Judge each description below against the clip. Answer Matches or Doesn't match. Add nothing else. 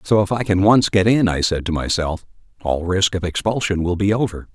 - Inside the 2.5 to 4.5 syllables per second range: Doesn't match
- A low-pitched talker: Matches